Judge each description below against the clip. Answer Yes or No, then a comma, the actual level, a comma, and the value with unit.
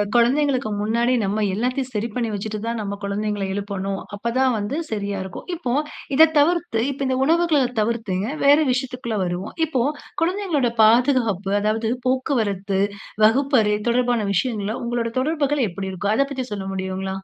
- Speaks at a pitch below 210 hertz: No, high, 230 Hz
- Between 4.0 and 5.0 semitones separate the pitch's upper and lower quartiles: Yes, average, 4.5 semitones